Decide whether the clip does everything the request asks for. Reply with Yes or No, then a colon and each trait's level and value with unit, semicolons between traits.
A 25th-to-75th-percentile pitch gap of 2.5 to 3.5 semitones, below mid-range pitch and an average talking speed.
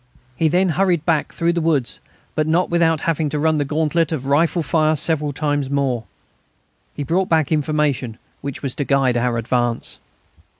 No: average, 3.1 semitones; medium, 150 Hz; average, 175 wpm